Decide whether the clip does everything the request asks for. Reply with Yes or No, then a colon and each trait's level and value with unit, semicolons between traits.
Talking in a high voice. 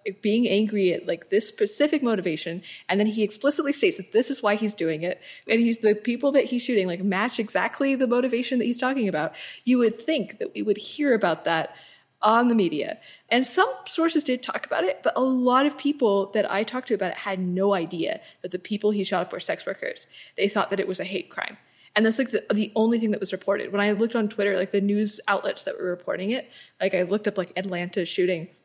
Yes: high, 210 Hz